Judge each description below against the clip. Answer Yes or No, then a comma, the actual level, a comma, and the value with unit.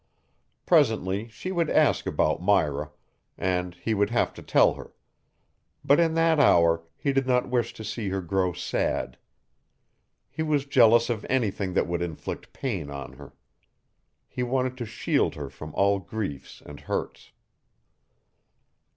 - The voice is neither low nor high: No, low, 105 Hz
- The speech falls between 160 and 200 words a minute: No, average, 150 wpm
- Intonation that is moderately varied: No, wide, 6.5 semitones